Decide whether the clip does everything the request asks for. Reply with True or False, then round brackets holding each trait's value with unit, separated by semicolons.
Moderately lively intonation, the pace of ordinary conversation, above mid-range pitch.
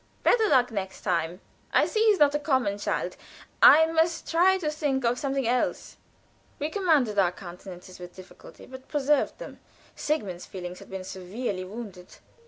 False (8.2 semitones; 165 wpm; 245 Hz)